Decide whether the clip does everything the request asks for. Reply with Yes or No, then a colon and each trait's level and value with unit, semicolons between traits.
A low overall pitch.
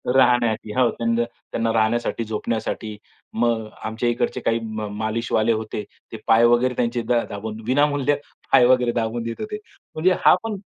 Yes: low, 115 Hz